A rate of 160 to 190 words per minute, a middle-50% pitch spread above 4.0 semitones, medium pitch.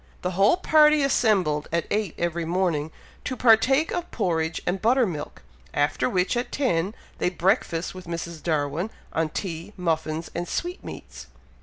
No: average, 150 wpm; wide, 5.5 semitones; medium, 180 Hz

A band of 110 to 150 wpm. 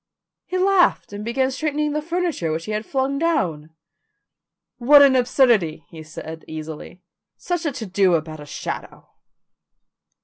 Yes: average, 145 wpm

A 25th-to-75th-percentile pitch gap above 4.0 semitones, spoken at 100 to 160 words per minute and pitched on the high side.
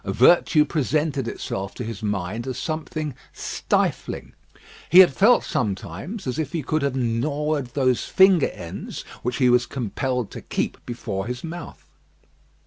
No: average, 5.1 semitones; average, 145 wpm; low, 130 Hz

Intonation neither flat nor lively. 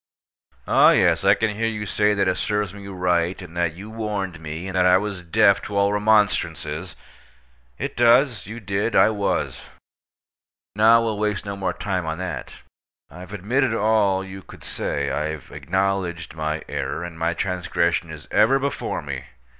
Yes: average, 3.5 semitones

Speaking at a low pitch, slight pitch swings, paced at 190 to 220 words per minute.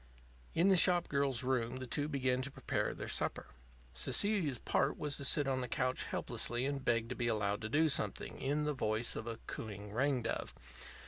No: low, 130 Hz; average, 3.7 semitones; average, 200 wpm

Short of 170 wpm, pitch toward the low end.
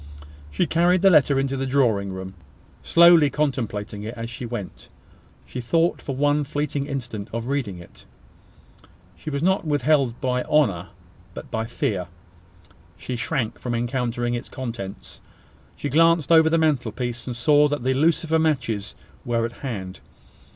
Yes: average, 150 wpm; low, 130 Hz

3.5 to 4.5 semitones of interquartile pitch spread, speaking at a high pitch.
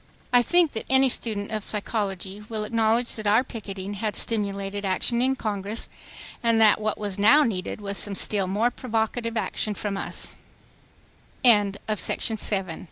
No: narrow, 2.4 semitones; high, 215 Hz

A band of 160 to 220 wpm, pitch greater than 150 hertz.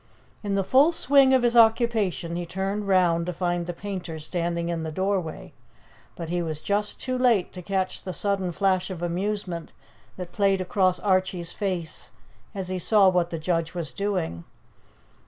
Yes: average, 175 wpm; medium, 185 Hz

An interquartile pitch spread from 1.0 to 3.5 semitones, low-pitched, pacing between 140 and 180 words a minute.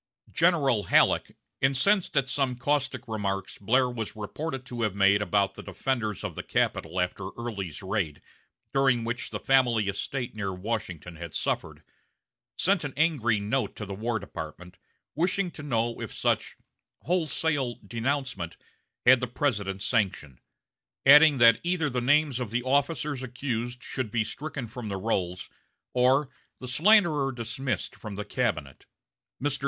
No: average, 4.9 semitones; low, 120 Hz; average, 150 wpm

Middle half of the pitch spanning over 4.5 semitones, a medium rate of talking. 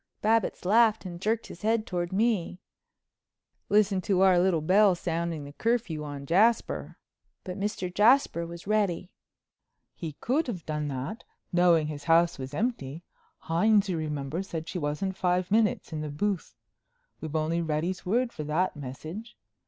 Yes: average, 4.9 semitones; average, 155 wpm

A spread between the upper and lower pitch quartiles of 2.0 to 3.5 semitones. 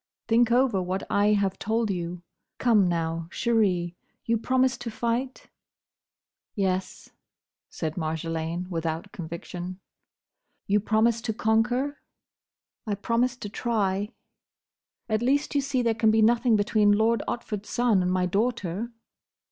No: average, 4.3 semitones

